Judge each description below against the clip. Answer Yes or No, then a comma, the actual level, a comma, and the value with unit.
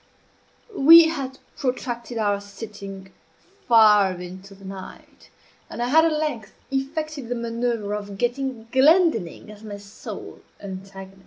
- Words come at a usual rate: No, slow, 130 wpm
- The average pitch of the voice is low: No, high, 225 Hz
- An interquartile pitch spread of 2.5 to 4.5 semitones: No, average, 5.2 semitones